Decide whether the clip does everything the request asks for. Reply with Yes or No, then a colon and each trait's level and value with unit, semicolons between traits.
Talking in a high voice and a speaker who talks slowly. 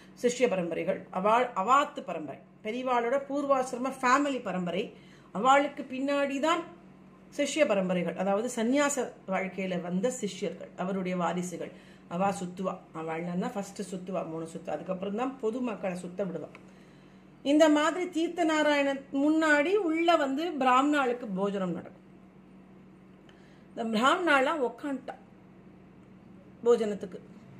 No: high, 230 Hz; average, 100 wpm